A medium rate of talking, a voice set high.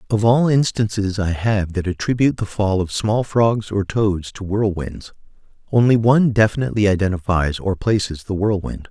No: average, 160 wpm; low, 105 Hz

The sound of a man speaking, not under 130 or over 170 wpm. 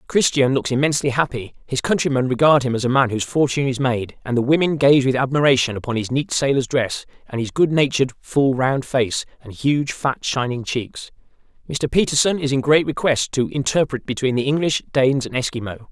No: male; average, 190 wpm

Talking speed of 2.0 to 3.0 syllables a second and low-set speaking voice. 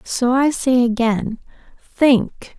No: 2.9 syllables/s; high, 245 Hz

